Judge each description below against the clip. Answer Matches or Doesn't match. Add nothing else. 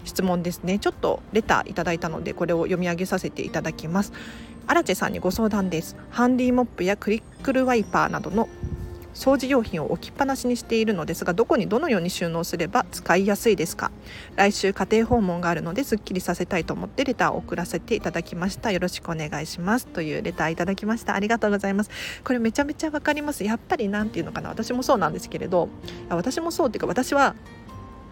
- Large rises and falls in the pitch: Doesn't match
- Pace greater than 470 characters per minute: Matches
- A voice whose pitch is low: Doesn't match